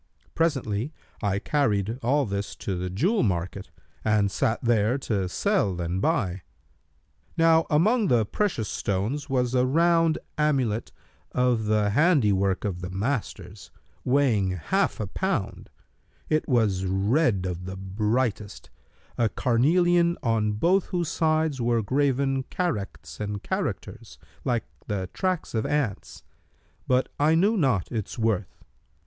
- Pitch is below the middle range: Yes, low, 120 Hz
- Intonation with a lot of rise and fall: Yes, wide, 6.8 semitones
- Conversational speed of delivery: No, slow, 130 wpm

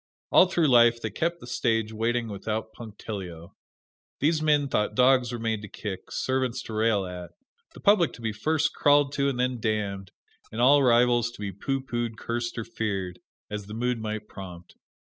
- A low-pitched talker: Yes, low, 115 Hz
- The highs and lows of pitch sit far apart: No, average, 3.5 semitones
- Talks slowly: No, average, 185 wpm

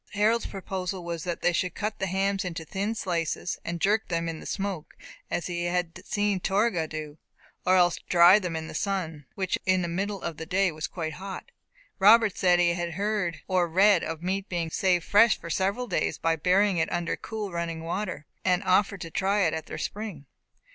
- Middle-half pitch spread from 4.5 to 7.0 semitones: No, average, 2.9 semitones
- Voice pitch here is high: No, medium, 180 Hz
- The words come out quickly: Yes, fast, 210 wpm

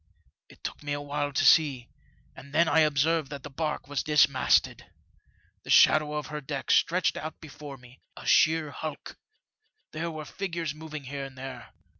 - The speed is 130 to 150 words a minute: No, average, 175 wpm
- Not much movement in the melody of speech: Yes, narrow, 2.1 semitones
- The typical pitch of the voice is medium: Yes, medium, 150 Hz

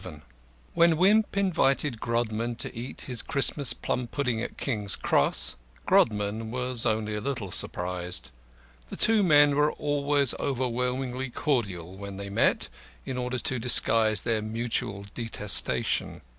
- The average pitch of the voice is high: No, low, 120 Hz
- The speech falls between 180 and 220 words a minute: No, slow, 135 wpm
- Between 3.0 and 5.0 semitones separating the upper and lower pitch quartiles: Yes, average, 4.4 semitones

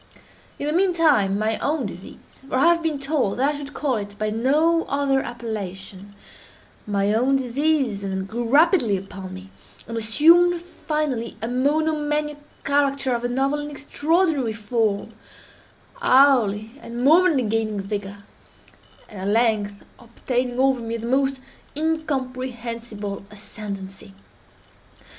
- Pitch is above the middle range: Yes, high, 245 Hz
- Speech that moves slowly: Yes, slow, 125 wpm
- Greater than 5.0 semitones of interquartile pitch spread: Yes, wide, 5.6 semitones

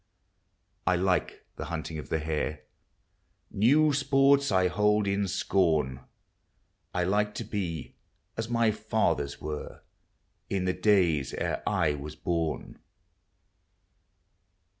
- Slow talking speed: Yes, slow, 115 wpm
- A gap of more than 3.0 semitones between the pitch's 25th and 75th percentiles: Yes, average, 5.0 semitones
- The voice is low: Yes, very low, 95 Hz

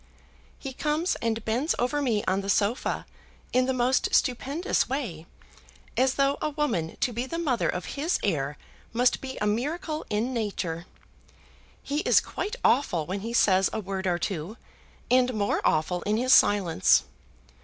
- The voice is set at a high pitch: Yes, high, 235 Hz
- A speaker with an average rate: Yes, average, 165 wpm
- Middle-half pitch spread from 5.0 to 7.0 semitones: Yes, wide, 5.5 semitones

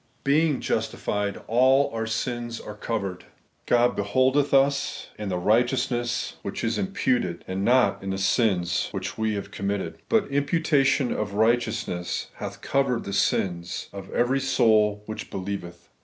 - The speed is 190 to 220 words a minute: No, average, 140 wpm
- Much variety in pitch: No, average, 5.0 semitones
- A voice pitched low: Yes, low, 115 Hz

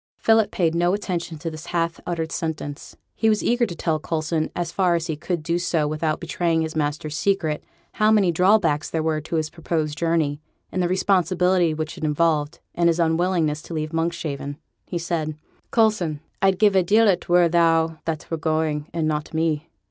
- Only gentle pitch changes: Yes, narrow, 2.2 semitones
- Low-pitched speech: No, medium, 165 Hz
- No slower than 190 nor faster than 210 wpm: Yes, average, 195 wpm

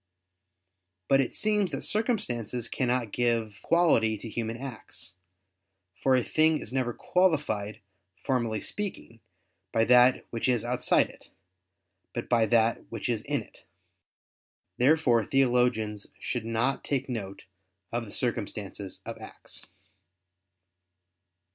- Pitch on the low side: Yes, low, 120 Hz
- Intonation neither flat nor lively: Yes, average, 3.3 semitones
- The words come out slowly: Yes, slow, 120 wpm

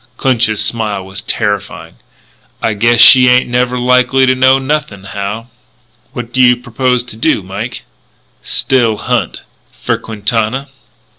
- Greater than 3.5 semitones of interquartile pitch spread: No, average, 2.9 semitones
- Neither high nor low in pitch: No, low, 120 Hz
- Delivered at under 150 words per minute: Yes, slow, 135 wpm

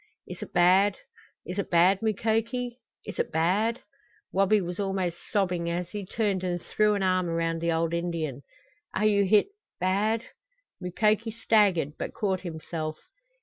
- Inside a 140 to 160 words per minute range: Yes, average, 155 wpm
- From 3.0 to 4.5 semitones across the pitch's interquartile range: Yes, average, 3.7 semitones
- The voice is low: No, high, 190 Hz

